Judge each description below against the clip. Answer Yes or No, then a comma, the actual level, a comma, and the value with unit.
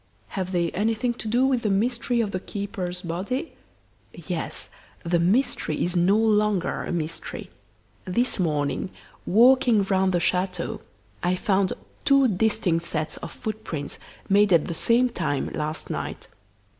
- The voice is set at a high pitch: Yes, high, 195 Hz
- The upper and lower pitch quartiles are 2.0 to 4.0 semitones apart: No, average, 4.4 semitones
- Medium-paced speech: Yes, average, 145 wpm